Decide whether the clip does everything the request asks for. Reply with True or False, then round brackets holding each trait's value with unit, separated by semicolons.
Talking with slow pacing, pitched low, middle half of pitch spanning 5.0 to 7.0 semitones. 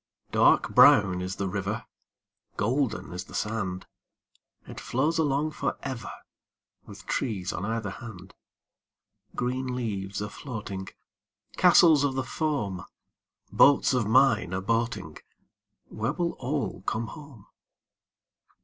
True (120 wpm; 115 Hz; 5.4 semitones)